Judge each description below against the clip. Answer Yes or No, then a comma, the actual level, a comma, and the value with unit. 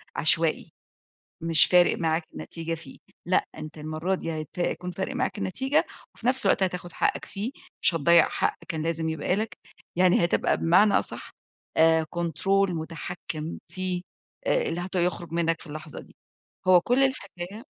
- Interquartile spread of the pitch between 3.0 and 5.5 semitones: No, narrow, 2.6 semitones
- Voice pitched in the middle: Yes, medium, 175 Hz